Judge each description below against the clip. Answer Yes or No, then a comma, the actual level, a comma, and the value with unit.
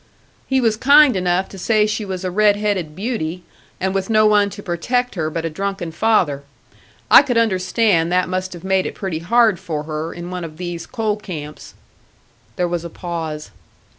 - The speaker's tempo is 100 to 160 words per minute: No, average, 195 wpm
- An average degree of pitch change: Yes, average, 3.9 semitones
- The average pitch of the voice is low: No, medium, 185 Hz